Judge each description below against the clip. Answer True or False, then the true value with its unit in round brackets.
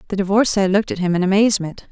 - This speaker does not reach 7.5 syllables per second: False (7.7 syllables/s)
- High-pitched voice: True (195 Hz)